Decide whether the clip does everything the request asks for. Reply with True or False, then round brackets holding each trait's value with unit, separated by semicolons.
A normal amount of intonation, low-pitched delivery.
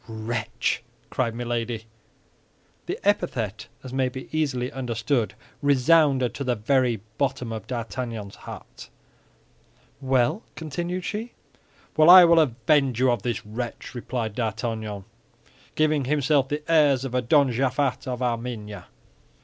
True (3.7 semitones; 125 Hz)